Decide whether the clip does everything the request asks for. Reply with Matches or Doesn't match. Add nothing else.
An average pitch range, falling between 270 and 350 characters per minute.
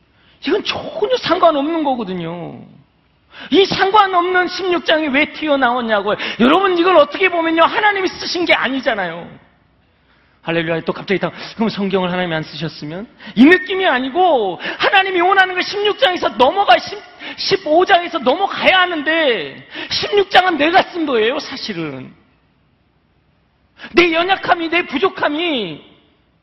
Doesn't match